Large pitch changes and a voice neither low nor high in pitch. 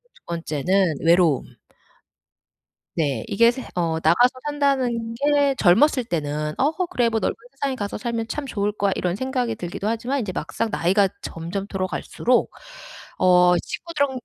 No: wide, 6.4 semitones; high, 210 Hz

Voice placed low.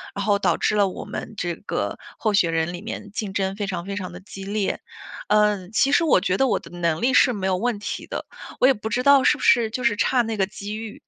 No: high, 205 Hz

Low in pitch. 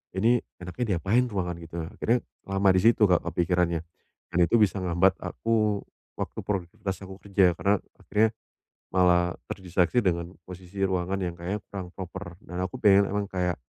Yes: very low, 95 Hz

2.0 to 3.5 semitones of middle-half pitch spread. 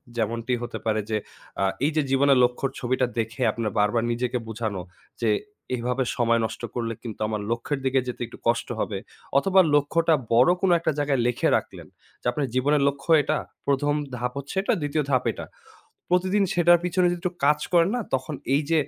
No: average, 4.6 semitones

